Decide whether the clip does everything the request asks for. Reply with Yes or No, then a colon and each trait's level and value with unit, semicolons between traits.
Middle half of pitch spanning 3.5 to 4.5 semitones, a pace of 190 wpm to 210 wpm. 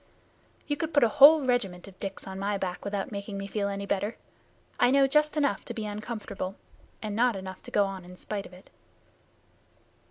Yes: average, 4.1 semitones; average, 200 wpm